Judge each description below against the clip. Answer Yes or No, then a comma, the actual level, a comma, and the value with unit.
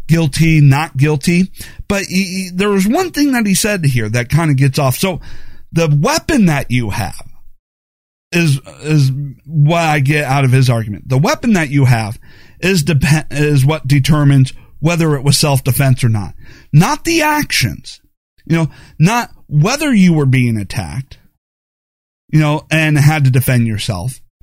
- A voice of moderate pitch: Yes, medium, 150 Hz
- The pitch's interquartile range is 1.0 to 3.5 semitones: No, average, 4.5 semitones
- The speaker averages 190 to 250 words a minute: No, average, 165 wpm